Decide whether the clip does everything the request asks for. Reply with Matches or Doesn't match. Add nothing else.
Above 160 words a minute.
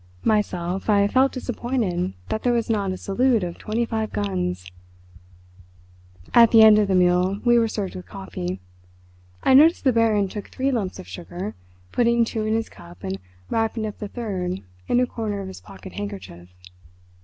Matches